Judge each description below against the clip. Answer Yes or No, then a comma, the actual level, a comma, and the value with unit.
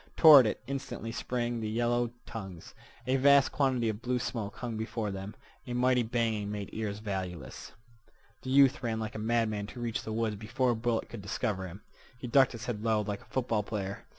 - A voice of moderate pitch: No, low, 115 Hz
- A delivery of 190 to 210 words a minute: Yes, average, 200 wpm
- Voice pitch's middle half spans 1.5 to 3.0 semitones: Yes, average, 2.7 semitones